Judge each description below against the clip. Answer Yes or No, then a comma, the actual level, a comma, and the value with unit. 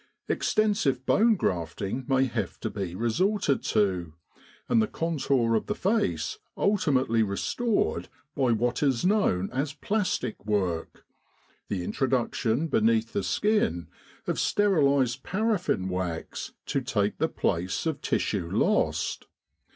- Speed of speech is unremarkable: No, slow, 120 wpm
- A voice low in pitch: Yes, low, 125 Hz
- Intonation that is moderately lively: No, wide, 8.8 semitones